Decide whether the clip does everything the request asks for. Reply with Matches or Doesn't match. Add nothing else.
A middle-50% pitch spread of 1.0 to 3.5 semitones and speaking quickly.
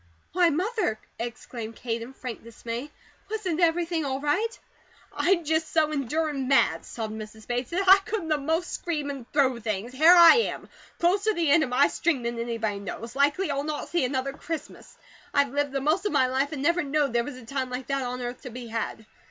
Doesn't match